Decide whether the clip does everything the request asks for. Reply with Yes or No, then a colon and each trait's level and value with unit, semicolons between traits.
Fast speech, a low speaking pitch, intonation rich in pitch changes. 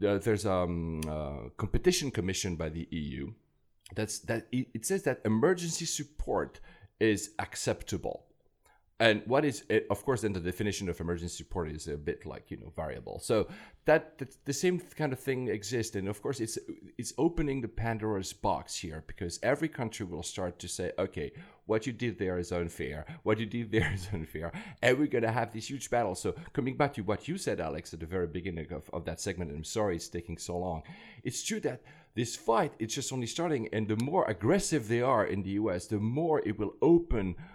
Yes: fast, 210 wpm; low, 110 Hz; wide, 6.7 semitones